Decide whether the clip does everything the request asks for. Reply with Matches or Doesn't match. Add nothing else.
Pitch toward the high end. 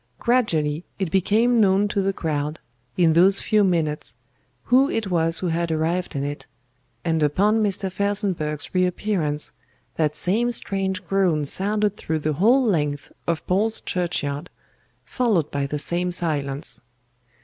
Doesn't match